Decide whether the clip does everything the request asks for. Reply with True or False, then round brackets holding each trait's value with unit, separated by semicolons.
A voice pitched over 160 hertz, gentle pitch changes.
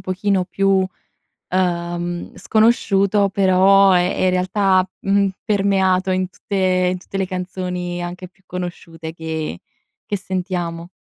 True (185 Hz; 1.7 semitones)